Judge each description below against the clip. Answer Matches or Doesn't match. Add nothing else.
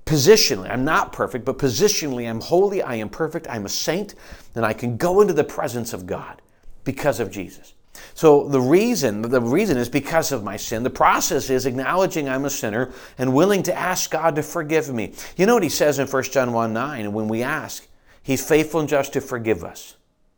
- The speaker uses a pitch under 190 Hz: Matches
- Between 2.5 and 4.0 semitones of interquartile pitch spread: Doesn't match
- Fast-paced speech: Matches